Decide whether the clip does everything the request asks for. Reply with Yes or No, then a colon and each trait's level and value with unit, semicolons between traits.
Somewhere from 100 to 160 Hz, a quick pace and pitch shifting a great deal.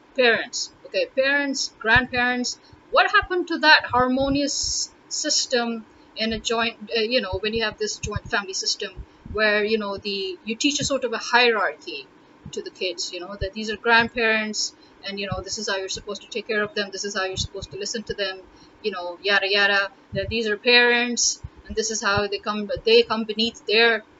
No: high, 230 Hz; fast, 210 wpm; wide, 5.8 semitones